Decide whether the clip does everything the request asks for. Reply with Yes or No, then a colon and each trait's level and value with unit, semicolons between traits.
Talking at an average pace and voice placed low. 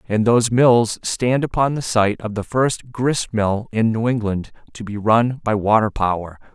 Yes: average, 190 wpm; low, 115 Hz